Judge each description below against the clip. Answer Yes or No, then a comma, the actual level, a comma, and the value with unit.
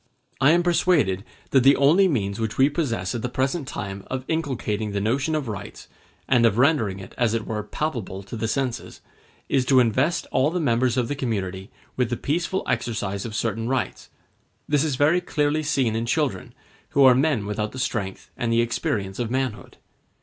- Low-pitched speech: Yes, low, 125 Hz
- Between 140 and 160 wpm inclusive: No, average, 195 wpm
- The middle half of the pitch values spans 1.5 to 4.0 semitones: No, average, 4.7 semitones